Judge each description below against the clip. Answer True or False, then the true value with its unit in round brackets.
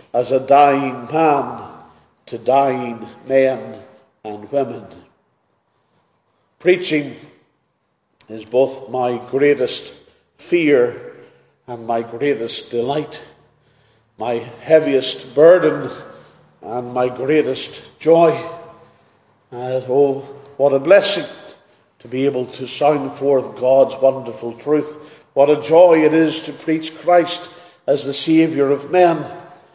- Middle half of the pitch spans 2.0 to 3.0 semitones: False (4.0 semitones)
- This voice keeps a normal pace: False (105 wpm)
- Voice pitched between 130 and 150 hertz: True (140 Hz)